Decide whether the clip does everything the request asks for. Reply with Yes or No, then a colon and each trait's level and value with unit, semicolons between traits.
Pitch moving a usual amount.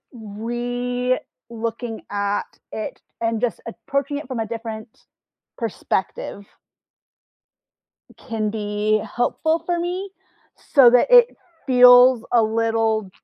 No: narrow, 2.3 semitones